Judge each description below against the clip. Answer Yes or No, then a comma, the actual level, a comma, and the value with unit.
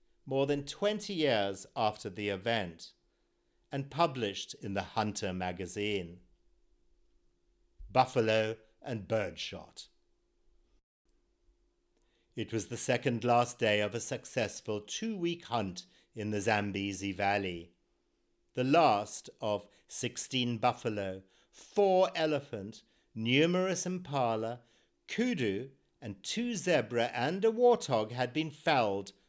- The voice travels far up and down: Yes, wide, 5.8 semitones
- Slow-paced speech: Yes, slow, 105 wpm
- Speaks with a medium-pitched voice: No, low, 115 Hz